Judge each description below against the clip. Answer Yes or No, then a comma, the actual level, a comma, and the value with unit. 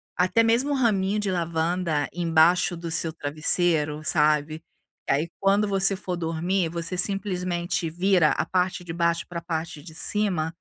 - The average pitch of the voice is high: No, medium, 175 Hz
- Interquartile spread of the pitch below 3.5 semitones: Yes, average, 2.8 semitones